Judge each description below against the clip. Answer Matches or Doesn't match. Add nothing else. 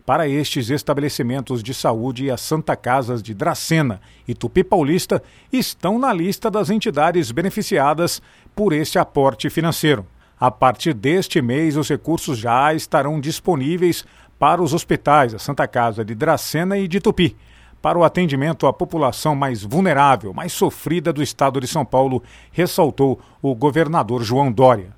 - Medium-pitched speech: Matches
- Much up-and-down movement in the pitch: Doesn't match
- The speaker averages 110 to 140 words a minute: Doesn't match